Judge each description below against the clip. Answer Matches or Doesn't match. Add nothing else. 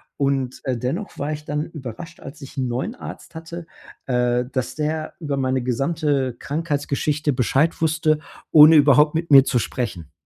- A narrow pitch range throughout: Doesn't match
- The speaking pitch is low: Doesn't match